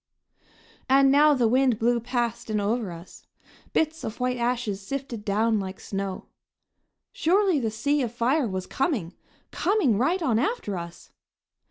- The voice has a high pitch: Yes, high, 240 Hz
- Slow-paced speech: No, average, 150 wpm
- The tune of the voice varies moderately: Yes, average, 4.8 semitones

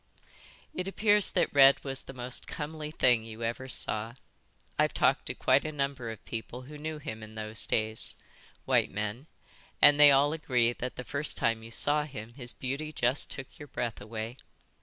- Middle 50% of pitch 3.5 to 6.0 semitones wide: Yes, average, 4.4 semitones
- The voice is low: Yes, low, 130 Hz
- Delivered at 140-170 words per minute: No, average, 185 wpm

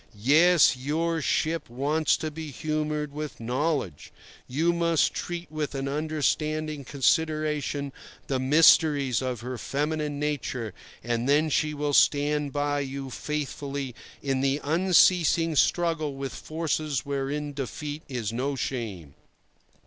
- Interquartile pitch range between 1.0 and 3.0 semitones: Yes, narrow, 2.4 semitones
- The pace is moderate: No, slow, 125 wpm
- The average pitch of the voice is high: No, medium, 145 Hz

